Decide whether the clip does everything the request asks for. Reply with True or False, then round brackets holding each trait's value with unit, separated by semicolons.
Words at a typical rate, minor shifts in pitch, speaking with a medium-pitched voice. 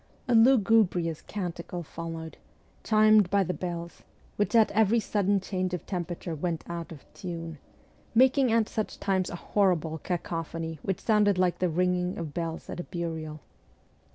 False (155 wpm; 3.6 semitones; 180 Hz)